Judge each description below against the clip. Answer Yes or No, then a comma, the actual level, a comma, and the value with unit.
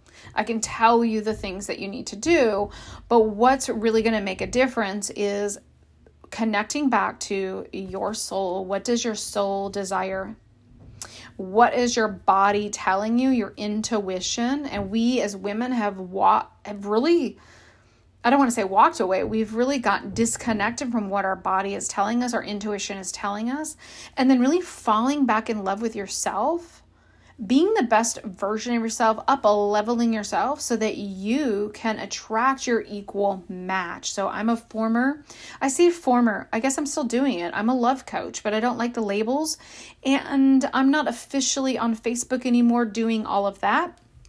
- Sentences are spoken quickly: No, average, 175 wpm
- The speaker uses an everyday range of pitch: Yes, average, 3.6 semitones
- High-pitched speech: Yes, high, 220 Hz